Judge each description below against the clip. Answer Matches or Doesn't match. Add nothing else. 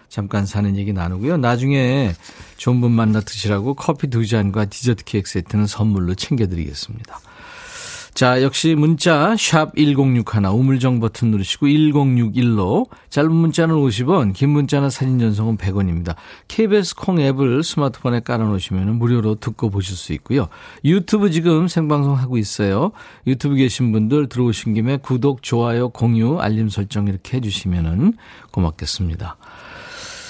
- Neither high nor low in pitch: Doesn't match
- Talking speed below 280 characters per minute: Doesn't match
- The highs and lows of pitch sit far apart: Matches